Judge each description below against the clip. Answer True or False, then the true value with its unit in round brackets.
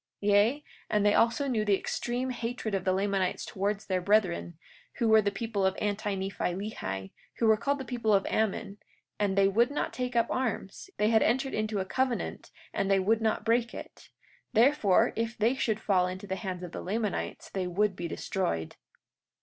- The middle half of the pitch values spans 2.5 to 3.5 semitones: True (3.1 semitones)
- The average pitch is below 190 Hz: False (210 Hz)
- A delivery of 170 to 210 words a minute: True (195 wpm)